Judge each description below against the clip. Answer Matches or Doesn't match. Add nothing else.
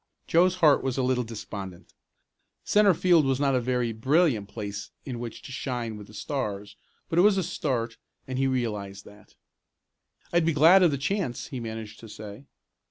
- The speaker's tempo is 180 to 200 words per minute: Matches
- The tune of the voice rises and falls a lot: Matches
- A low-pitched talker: Matches